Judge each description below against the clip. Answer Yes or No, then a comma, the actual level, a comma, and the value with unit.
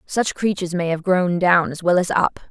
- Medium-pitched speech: Yes, medium, 180 Hz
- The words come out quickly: Yes, fast, 240 wpm